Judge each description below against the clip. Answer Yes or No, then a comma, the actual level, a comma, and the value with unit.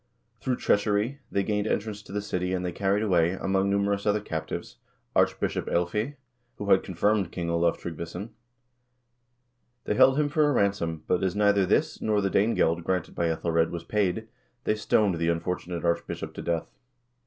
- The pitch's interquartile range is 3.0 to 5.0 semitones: Yes, average, 3.4 semitones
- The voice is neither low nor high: No, very low, 95 Hz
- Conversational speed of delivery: Yes, average, 175 wpm